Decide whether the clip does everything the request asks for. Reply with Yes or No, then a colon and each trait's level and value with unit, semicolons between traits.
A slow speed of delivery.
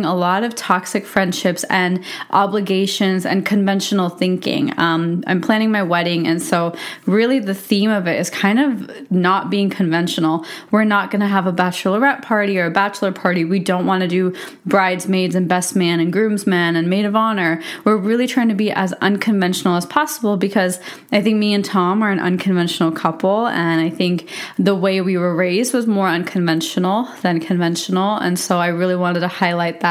No: average, 190 wpm